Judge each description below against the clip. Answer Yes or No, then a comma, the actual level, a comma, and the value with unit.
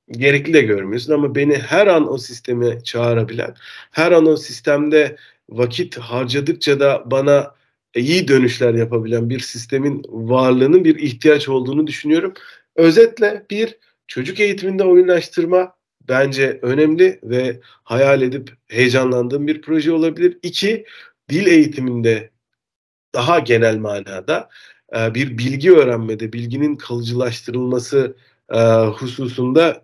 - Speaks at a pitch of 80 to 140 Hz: Yes, low, 135 Hz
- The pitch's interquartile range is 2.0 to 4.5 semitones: No, average, 4.9 semitones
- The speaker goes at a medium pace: Yes, average, 110 wpm